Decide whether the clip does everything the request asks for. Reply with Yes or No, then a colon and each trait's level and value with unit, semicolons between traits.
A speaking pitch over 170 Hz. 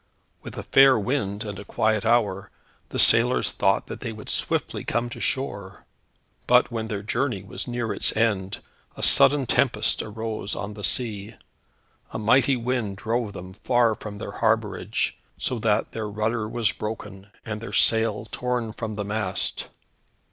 No: low, 110 Hz